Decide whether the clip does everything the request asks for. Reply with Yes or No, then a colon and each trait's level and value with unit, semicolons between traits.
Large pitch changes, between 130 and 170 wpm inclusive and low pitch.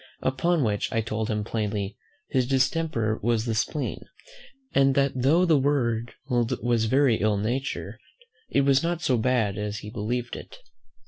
No: average, 4.0 semitones; average, 155 wpm; low, 120 Hz